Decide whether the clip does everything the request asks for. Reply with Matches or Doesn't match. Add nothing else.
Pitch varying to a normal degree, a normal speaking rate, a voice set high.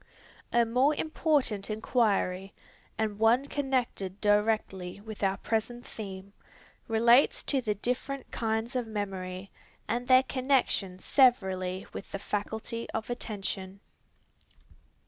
Doesn't match